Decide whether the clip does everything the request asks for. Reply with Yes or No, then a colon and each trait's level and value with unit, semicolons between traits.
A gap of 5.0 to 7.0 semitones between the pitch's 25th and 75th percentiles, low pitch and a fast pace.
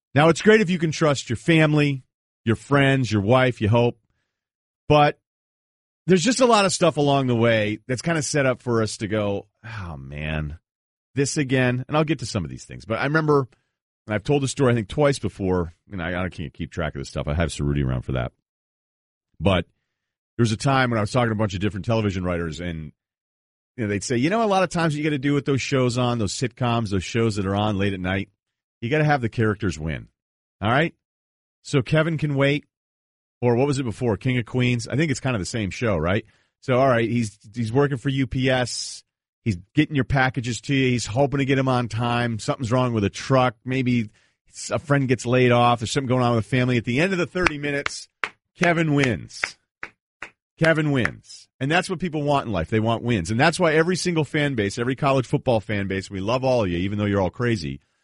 Yes: average, 5.3 semitones; low, 120 Hz; fast, 240 wpm